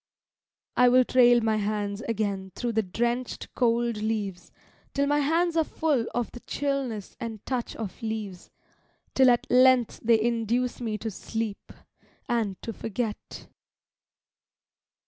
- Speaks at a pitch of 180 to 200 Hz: No, high, 230 Hz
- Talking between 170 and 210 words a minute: No, slow, 135 wpm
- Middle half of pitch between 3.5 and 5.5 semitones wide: No, average, 2.7 semitones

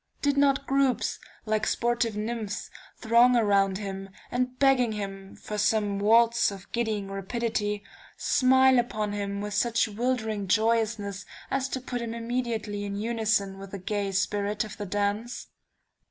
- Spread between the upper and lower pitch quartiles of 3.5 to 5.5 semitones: No, average, 2.9 semitones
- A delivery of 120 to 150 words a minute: Yes, average, 145 wpm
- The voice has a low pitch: No, high, 215 Hz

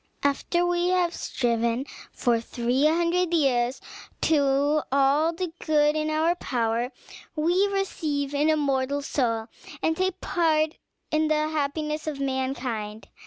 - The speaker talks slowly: Yes, slow, 125 wpm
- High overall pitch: Yes, very high, 300 Hz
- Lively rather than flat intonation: No, average, 3.6 semitones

